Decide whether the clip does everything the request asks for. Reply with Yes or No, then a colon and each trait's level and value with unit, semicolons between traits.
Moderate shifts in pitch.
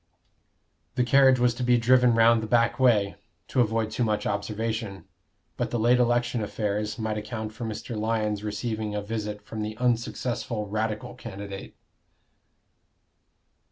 No: narrow, 2.1 semitones